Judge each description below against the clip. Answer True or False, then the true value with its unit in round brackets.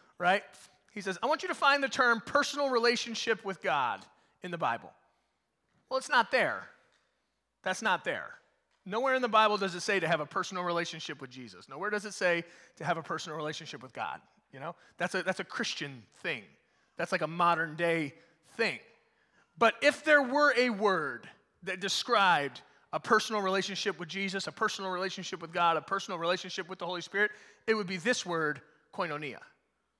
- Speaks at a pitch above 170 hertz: True (190 Hz)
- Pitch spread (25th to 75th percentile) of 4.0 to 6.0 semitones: True (4.9 semitones)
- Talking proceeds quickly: False (190 wpm)